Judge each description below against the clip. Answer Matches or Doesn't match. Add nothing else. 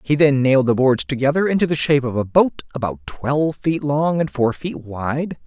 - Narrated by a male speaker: Matches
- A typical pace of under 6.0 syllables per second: Matches